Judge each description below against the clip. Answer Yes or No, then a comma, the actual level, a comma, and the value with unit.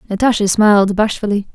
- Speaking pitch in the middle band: No, high, 210 Hz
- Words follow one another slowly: Yes, slow, 115 wpm